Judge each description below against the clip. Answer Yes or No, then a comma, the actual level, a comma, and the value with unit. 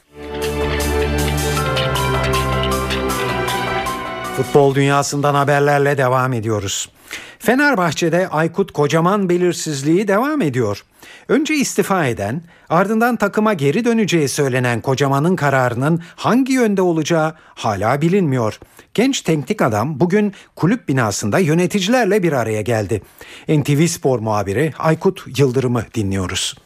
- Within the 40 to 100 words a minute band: Yes, slow, 95 wpm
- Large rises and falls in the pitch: Yes, wide, 8.1 semitones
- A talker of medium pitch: Yes, medium, 145 Hz